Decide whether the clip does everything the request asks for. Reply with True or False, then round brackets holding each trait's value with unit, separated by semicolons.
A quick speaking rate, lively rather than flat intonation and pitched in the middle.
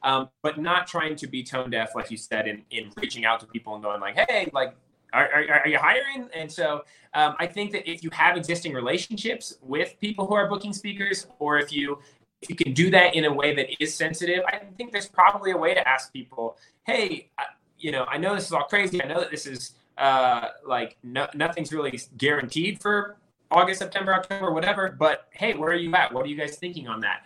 True (235 wpm; 5.9 semitones; 160 Hz)